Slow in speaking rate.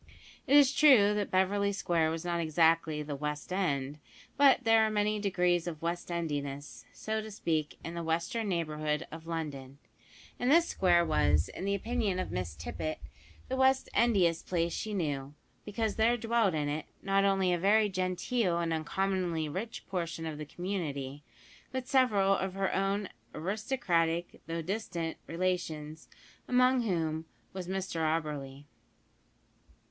No: average, 150 wpm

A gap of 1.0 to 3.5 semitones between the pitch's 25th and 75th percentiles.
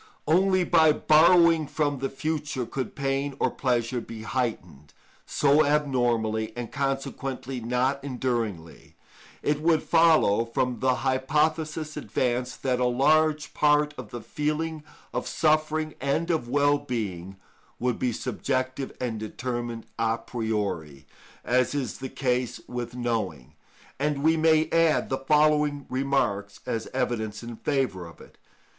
No: average, 4.1 semitones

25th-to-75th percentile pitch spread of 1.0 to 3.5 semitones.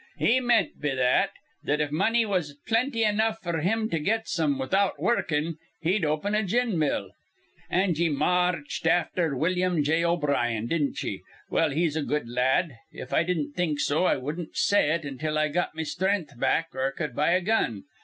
No: average, 4.1 semitones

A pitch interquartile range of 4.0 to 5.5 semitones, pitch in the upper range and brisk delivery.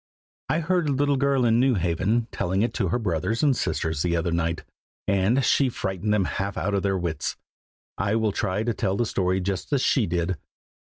No: average, 5.0 semitones; low, 100 Hz; fast, 210 wpm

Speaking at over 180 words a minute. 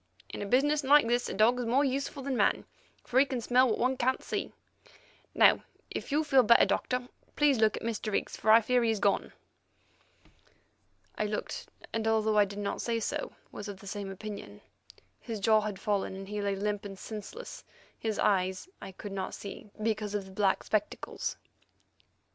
Yes: average, 190 wpm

